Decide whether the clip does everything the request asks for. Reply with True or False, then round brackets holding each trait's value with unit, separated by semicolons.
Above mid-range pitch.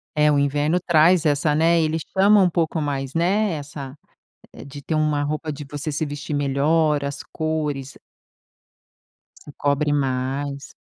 False (150 Hz)